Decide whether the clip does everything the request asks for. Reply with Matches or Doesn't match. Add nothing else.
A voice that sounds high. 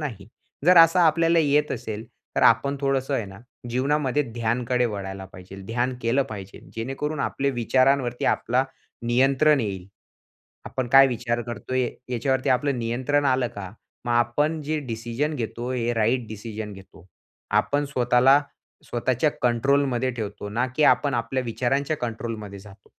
Doesn't match